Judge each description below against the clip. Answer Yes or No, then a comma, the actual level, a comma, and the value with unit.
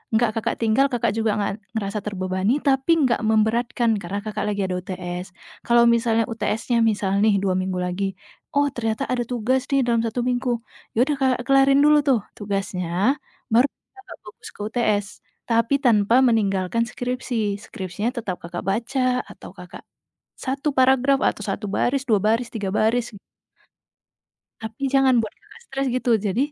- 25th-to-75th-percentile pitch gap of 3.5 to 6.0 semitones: Yes, average, 3.9 semitones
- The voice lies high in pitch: Yes, high, 230 Hz